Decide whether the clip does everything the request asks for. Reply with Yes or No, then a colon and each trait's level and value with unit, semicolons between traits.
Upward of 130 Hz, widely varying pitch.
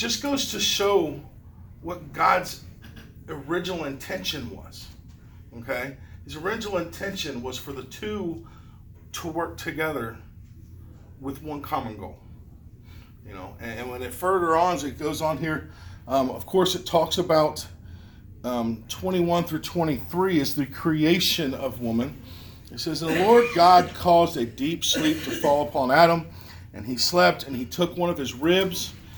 Yes: medium, 140 Hz; wide, 7.8 semitones